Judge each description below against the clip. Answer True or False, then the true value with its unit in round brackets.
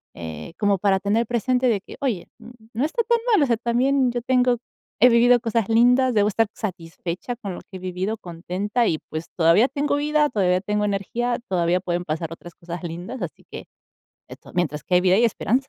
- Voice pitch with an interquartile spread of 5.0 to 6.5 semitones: True (5.4 semitones)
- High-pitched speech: True (210 Hz)